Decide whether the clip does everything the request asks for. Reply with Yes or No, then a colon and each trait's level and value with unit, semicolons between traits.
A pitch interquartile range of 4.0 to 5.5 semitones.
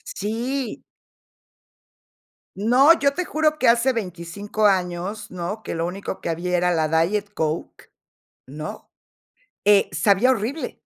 Yes: average, 5.1 semitones